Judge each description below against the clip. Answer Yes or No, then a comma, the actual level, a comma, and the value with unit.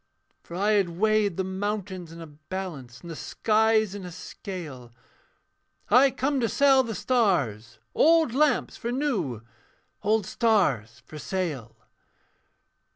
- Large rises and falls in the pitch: Yes, wide, 5.7 semitones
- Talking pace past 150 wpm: No, slow, 135 wpm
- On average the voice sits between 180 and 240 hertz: Yes, high, 190 Hz